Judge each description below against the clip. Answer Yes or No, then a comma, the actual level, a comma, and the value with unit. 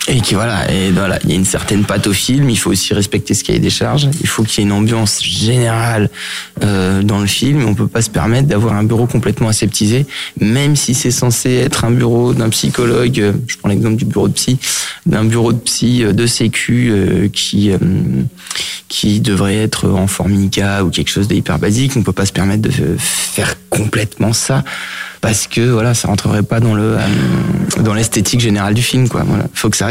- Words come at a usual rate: No, fast, 225 wpm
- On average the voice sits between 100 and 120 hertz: Yes, low, 110 Hz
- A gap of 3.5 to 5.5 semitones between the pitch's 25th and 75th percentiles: No, average, 2.8 semitones